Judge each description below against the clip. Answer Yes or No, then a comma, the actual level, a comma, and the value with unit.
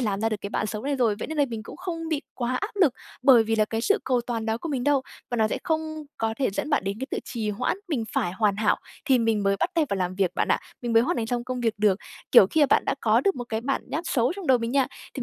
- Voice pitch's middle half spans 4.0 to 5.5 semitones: Yes, average, 4.6 semitones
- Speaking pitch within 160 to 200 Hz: No, high, 240 Hz